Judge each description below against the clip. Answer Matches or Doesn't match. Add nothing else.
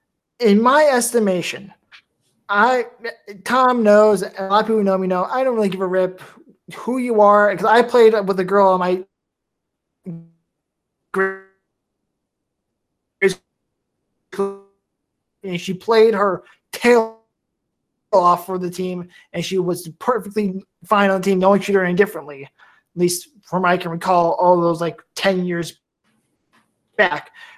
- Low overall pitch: Doesn't match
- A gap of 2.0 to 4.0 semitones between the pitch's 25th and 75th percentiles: Matches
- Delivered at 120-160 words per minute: Matches